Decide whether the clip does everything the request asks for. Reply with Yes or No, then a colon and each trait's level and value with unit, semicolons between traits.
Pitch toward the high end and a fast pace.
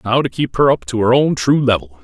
No: low, 125 Hz; fast, 295 wpm